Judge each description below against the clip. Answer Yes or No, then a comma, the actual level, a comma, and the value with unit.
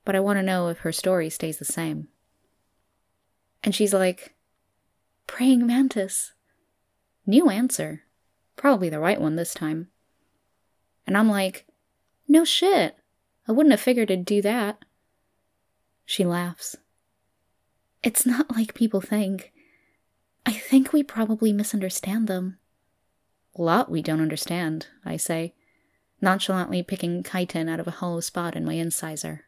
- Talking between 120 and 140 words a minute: Yes, slow, 135 wpm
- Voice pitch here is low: No, medium, 185 Hz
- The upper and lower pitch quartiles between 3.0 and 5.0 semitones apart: No, wide, 5.6 semitones